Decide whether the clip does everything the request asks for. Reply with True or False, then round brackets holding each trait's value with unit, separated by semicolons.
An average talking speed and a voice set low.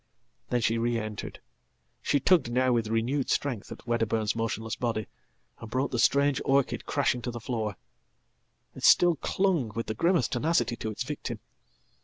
True (155 wpm; 120 Hz)